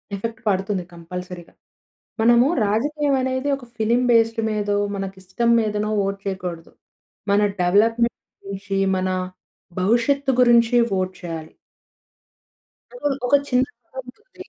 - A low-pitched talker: No, high, 215 Hz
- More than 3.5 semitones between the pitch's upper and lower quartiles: Yes, average, 4.0 semitones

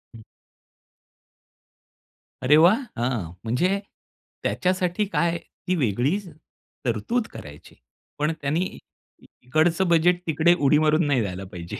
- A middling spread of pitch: No, wide, 6.3 semitones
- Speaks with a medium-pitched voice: Yes, medium, 155 Hz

